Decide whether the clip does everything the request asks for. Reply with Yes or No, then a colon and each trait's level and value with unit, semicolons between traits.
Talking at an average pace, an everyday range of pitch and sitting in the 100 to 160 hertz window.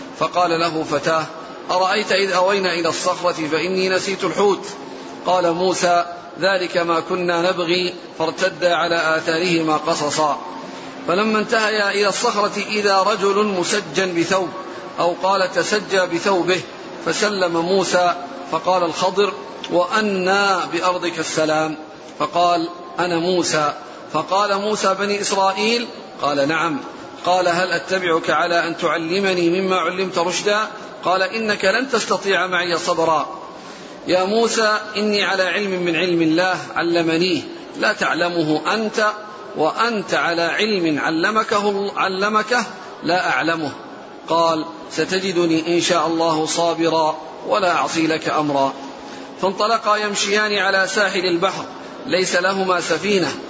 No: average, 115 wpm; average, 3.0 semitones; medium, 180 Hz